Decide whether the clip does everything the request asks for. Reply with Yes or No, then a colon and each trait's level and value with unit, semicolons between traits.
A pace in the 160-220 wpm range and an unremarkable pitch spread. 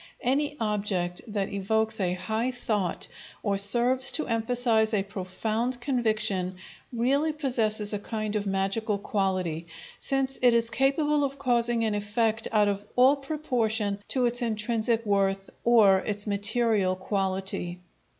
No: slow, 135 wpm; average, 3.5 semitones